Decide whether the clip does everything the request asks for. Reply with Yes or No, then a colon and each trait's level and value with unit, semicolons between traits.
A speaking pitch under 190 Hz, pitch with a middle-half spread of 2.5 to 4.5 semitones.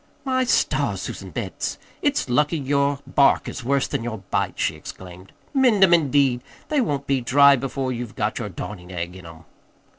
No: low, 135 Hz; average, 5.1 semitones